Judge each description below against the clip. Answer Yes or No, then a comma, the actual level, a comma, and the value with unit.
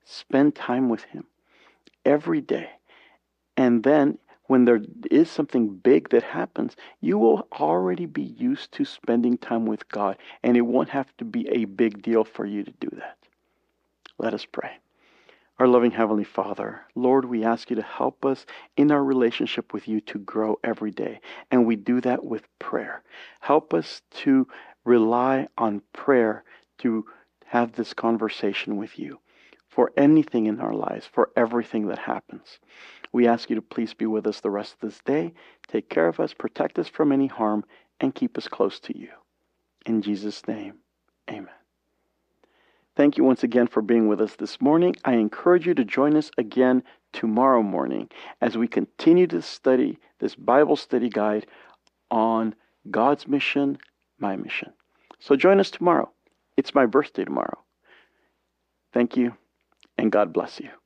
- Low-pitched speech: Yes, low, 120 Hz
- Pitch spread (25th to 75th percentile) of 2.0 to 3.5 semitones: No, average, 3.9 semitones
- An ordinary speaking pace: Yes, average, 165 wpm